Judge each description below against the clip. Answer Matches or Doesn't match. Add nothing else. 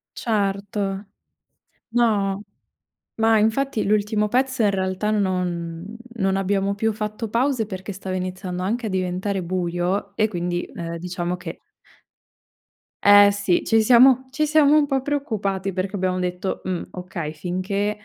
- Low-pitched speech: Doesn't match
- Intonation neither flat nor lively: Matches